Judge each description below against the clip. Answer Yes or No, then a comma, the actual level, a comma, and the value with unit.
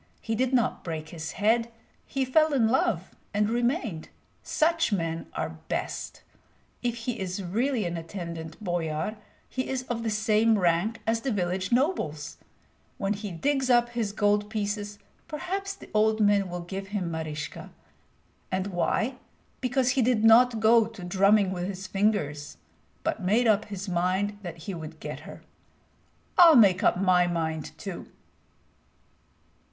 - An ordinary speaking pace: Yes, average, 155 wpm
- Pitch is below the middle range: No, high, 205 Hz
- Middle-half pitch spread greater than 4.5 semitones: Yes, average, 5.0 semitones